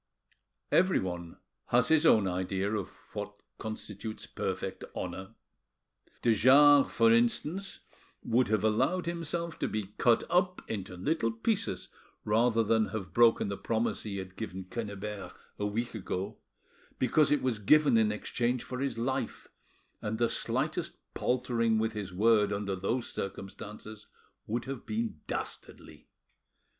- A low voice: Yes, low, 115 Hz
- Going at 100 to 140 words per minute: Yes, slow, 135 wpm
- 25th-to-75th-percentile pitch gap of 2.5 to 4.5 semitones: Yes, average, 3.9 semitones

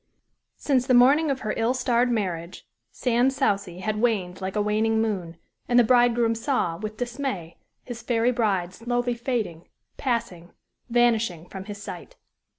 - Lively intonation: No, average, 3.9 semitones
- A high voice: Yes, high, 230 Hz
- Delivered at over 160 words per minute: No, average, 155 wpm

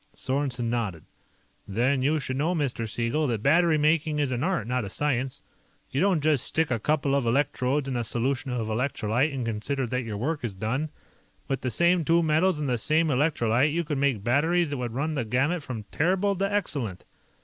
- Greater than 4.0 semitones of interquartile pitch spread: Yes, average, 4.4 semitones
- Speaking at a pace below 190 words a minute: No, fast, 205 wpm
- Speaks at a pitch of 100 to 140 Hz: Yes, low, 135 Hz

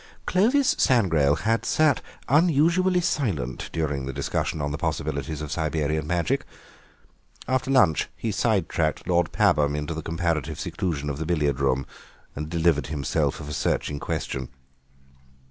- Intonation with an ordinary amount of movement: No, wide, 6.9 semitones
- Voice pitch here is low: Yes, very low, 80 Hz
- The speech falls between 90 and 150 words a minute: Yes, average, 145 wpm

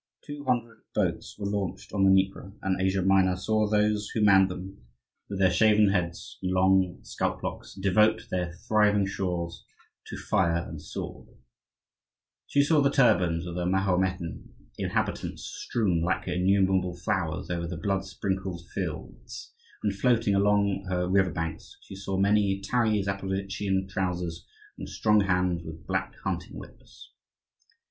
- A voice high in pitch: No, very low, 95 Hz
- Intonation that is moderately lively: No, narrow, 2.2 semitones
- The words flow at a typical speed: Yes, average, 150 wpm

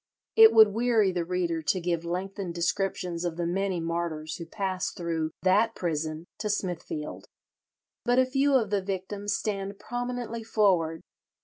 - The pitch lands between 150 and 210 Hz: Yes, high, 190 Hz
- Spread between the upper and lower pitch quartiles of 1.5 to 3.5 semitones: No, average, 3.9 semitones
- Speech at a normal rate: Yes, average, 150 wpm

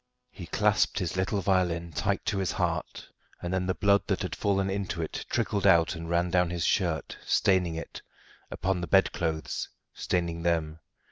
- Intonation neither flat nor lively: No, narrow, 2.3 semitones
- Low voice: Yes, very low, 90 Hz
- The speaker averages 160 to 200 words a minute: Yes, average, 175 wpm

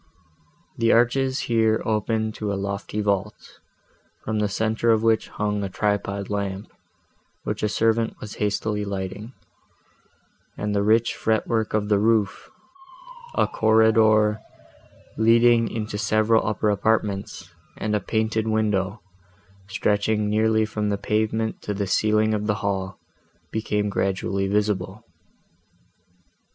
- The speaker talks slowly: Yes, slow, 125 wpm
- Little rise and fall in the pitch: Yes, narrow, 1.4 semitones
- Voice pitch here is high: No, low, 105 Hz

